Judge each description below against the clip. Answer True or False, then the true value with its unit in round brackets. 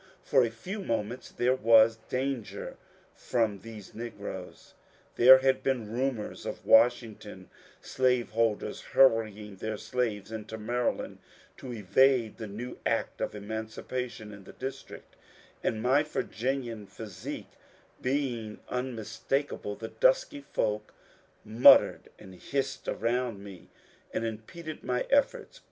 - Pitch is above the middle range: False (115 Hz)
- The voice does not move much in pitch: False (3.2 semitones)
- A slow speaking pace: True (120 wpm)